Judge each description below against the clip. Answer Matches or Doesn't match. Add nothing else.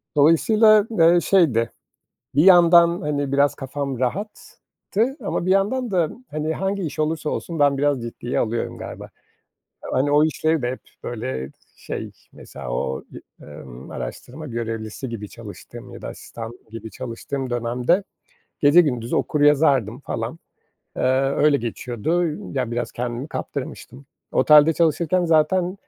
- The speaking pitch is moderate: Matches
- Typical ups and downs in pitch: Doesn't match